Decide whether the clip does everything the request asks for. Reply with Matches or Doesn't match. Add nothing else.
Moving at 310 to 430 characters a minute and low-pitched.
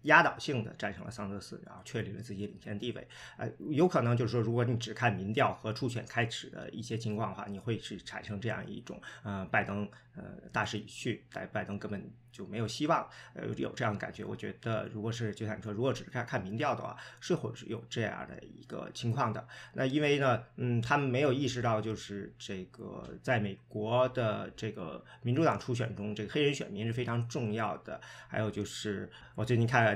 Matches